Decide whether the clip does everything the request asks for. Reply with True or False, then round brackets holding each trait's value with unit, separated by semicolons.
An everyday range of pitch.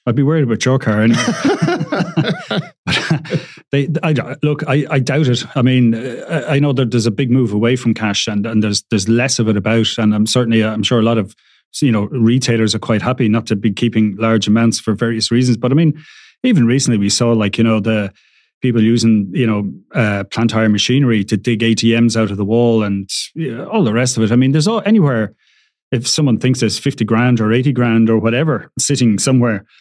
True (3.0 semitones)